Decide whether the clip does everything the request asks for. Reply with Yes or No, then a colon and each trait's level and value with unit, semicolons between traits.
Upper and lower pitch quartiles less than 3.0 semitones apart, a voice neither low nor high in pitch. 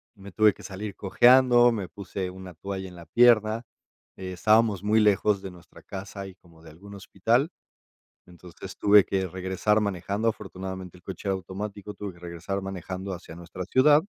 No: narrow, 2.4 semitones; very low, 95 Hz